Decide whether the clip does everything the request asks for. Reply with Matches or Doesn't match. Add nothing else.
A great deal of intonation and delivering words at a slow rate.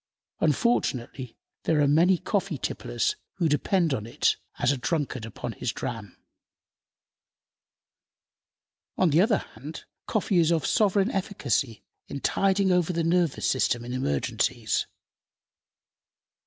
Matches